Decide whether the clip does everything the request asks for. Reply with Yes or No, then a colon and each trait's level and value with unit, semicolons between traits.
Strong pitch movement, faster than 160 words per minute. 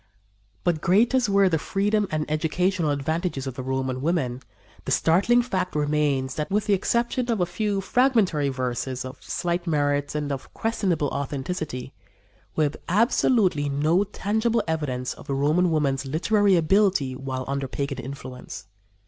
No: wide, 6.0 semitones; average, 155 wpm